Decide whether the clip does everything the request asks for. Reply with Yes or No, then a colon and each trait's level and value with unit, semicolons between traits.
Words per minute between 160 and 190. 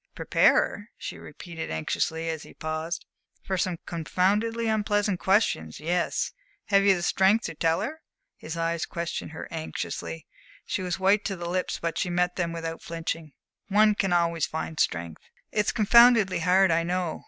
Yes: average, 165 wpm